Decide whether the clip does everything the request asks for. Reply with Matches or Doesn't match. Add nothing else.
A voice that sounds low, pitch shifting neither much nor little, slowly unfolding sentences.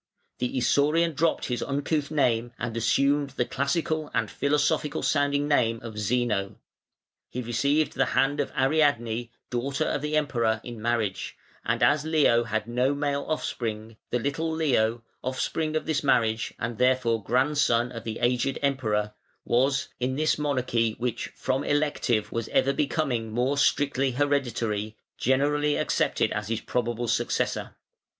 Doesn't match